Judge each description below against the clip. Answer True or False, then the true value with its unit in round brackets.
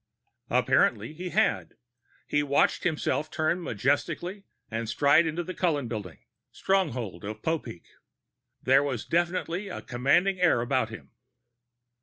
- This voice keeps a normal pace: False (130 wpm)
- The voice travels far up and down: True (6.6 semitones)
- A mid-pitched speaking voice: True (145 Hz)